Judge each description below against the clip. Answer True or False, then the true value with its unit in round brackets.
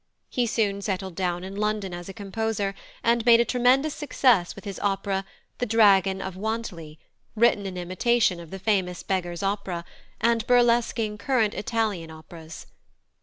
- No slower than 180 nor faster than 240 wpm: False (155 wpm)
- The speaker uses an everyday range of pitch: True (3.6 semitones)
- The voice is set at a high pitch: True (200 Hz)